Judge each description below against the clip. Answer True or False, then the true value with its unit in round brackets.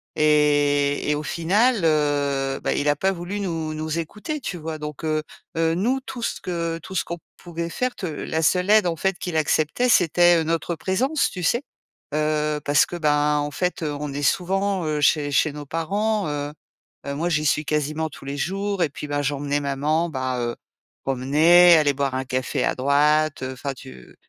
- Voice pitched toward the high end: False (155 Hz)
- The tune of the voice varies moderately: True (3.3 semitones)